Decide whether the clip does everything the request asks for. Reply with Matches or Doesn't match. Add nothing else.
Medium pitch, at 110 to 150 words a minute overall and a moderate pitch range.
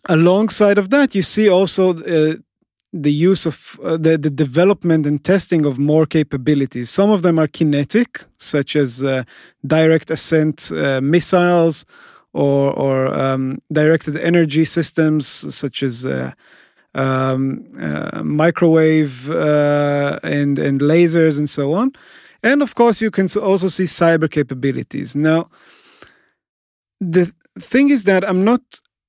Matches